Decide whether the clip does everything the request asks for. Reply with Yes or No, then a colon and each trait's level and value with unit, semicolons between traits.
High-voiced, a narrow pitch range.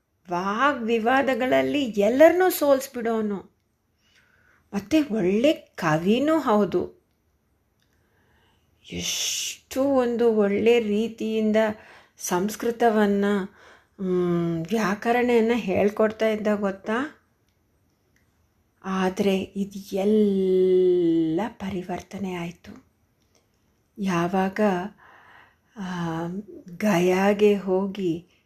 No: high, 200 Hz; average, 4.2 semitones